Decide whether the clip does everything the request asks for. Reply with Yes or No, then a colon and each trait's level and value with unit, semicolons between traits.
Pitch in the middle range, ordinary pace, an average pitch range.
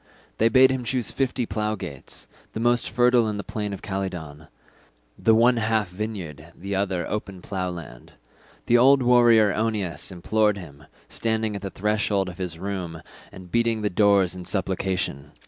No: low, 100 Hz; average, 170 wpm; average, 3.7 semitones